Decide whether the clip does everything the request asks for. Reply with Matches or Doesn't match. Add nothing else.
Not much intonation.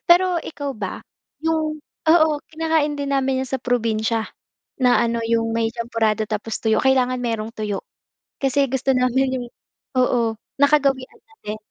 Doesn't match